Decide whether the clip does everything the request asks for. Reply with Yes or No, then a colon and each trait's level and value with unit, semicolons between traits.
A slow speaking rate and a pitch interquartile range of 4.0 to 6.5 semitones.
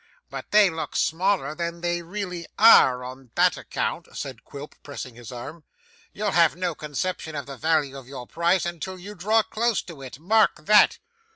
No: average, 180 wpm; average, 5.2 semitones